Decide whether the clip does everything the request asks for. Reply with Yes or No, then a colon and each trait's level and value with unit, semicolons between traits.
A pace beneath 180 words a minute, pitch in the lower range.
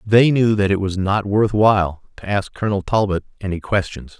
No: average, 200 wpm; low, 100 Hz